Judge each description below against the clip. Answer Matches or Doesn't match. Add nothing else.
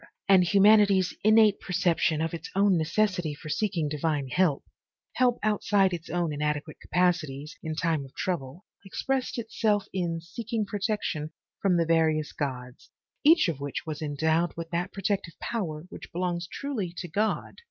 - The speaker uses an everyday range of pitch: Matches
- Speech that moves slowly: Doesn't match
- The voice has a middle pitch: Matches